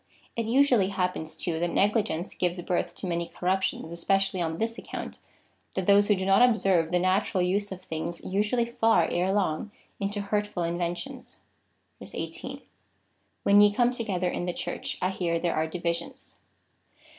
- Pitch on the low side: No, high, 190 Hz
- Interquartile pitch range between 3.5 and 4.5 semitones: No, average, 3.1 semitones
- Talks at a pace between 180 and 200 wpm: No, average, 170 wpm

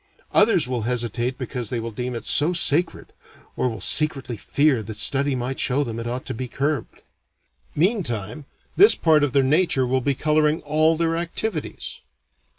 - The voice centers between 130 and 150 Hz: Yes, low, 135 Hz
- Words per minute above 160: Yes, average, 170 wpm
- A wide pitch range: No, average, 4.2 semitones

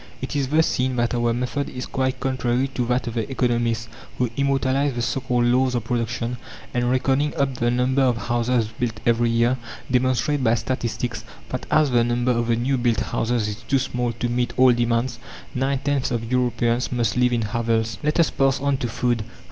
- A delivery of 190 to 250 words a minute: Yes, fast, 205 wpm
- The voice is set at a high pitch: No, low, 125 Hz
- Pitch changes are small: Yes, narrow, 1.8 semitones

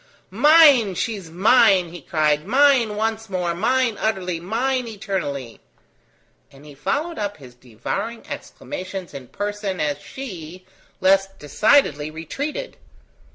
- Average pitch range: No, wide, 6.3 semitones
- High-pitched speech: Yes, high, 195 Hz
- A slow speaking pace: Yes, slow, 120 wpm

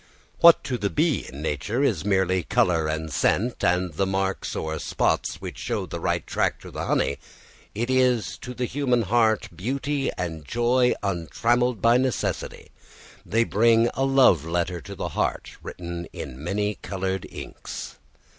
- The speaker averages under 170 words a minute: Yes, average, 155 wpm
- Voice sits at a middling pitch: No, low, 105 Hz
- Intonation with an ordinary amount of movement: No, wide, 6.1 semitones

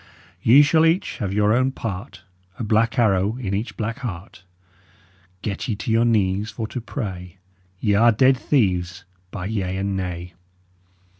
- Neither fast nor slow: Yes, average, 160 wpm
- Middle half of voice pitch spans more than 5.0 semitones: No, average, 3.8 semitones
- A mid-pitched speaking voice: No, low, 105 Hz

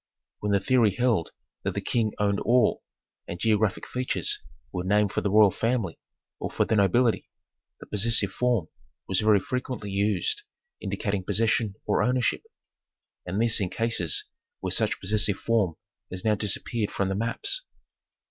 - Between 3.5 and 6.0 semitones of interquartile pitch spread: No, average, 2.9 semitones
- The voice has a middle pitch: No, low, 105 Hz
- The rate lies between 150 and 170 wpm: Yes, average, 155 wpm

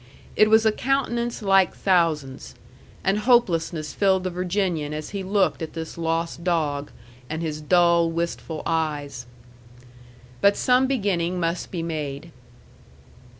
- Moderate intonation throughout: Yes, average, 3.6 semitones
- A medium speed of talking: No, slow, 130 wpm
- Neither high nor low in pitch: Yes, medium, 170 Hz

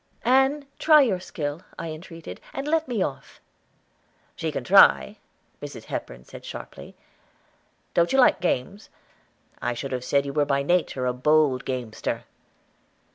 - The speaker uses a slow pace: No, average, 145 wpm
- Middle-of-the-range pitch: Yes, medium, 155 Hz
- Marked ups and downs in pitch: Yes, wide, 8.3 semitones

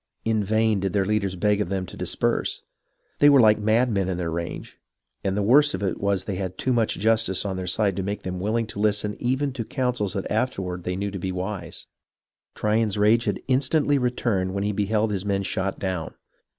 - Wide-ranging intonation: No, average, 2.8 semitones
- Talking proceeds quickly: Yes, fast, 215 wpm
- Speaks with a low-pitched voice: Yes, low, 105 Hz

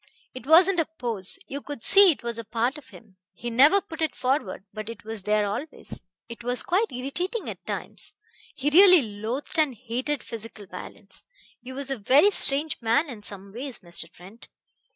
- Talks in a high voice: Yes, very high, 255 Hz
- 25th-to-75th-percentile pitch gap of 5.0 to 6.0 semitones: Yes, average, 5.3 semitones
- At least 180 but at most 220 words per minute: Yes, average, 190 wpm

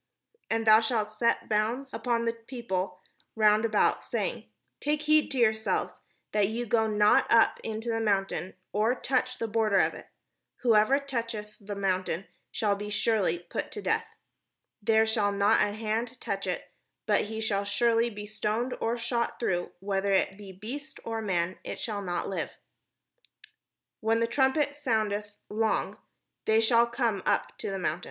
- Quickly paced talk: No, average, 170 wpm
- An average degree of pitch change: No, narrow, 2.2 semitones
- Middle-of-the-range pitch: No, high, 220 Hz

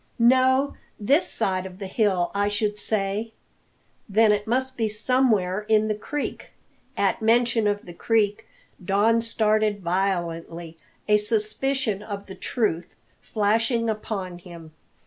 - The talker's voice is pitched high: Yes, high, 210 Hz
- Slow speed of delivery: Yes, slow, 130 wpm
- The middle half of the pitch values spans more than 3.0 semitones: No, average, 2.7 semitones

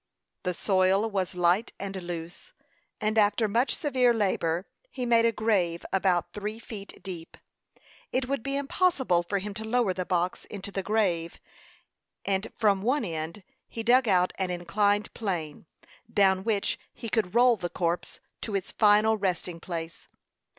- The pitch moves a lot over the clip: No, average, 3.8 semitones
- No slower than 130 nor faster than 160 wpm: Yes, average, 155 wpm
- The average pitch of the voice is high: Yes, high, 200 Hz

